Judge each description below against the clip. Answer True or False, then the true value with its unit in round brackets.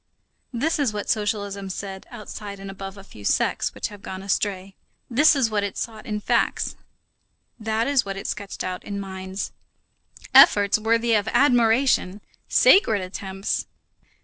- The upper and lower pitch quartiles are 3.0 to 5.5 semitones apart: False (2.6 semitones)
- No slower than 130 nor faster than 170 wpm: True (150 wpm)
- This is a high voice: True (205 Hz)